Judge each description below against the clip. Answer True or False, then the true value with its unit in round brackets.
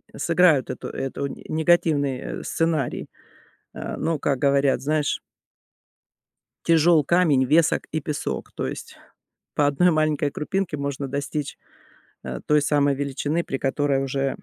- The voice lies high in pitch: False (145 Hz)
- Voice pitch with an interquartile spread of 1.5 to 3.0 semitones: True (2.4 semitones)